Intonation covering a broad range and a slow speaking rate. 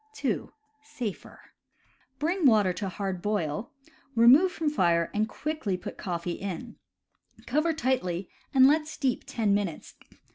Yes: wide, 8.0 semitones; slow, 130 wpm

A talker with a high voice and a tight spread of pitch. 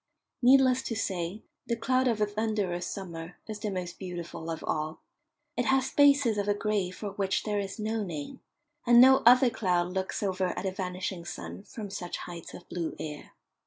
No: high, 200 Hz; average, 4.2 semitones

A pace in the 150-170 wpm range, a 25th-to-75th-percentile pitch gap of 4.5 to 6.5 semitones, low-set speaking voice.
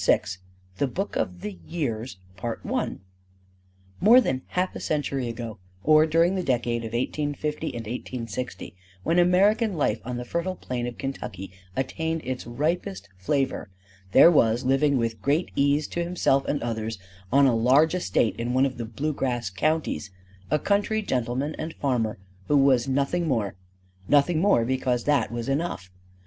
Yes: average, 155 wpm; average, 5.1 semitones; low, 130 Hz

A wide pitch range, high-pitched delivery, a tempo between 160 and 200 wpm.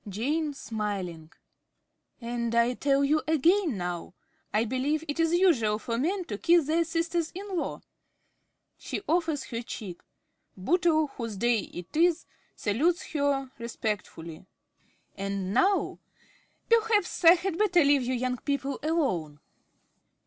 No: wide, 7.3 semitones; very high, 280 Hz; slow, 135 wpm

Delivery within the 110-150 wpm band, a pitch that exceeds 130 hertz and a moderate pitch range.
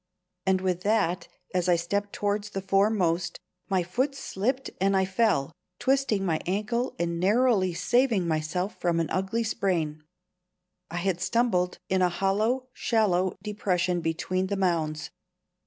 Yes: average, 140 wpm; high, 190 Hz; average, 3.3 semitones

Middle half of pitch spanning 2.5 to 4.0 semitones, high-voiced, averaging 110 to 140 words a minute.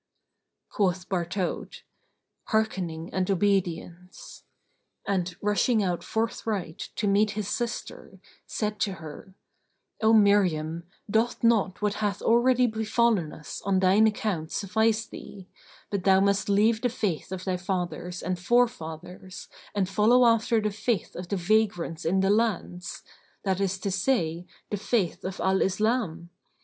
Yes: average, 3.3 semitones; high, 195 Hz; slow, 135 wpm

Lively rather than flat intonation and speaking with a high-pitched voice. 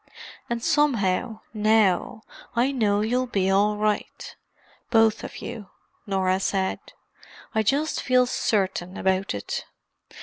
No: average, 3.6 semitones; high, 215 Hz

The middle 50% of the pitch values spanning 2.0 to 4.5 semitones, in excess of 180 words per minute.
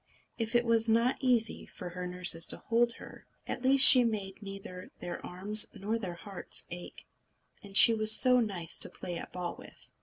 Yes: average, 4.2 semitones; average, 190 wpm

